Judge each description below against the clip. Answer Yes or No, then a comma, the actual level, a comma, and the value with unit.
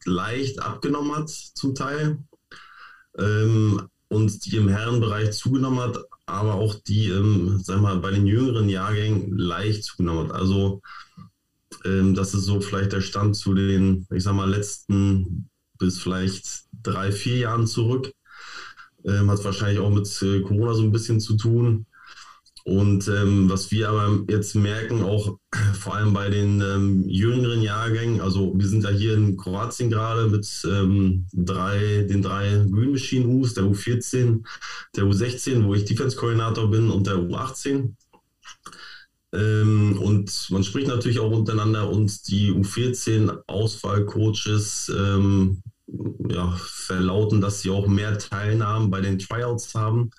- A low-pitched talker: Yes, low, 105 Hz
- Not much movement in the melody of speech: Yes, narrow, 2.3 semitones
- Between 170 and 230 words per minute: No, average, 145 wpm